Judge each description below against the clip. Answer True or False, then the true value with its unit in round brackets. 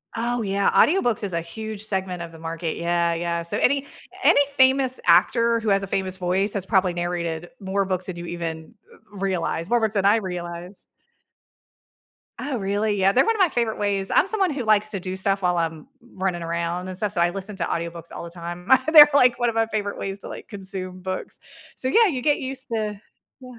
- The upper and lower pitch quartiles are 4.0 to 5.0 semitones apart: True (4.5 semitones)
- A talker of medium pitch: False (195 Hz)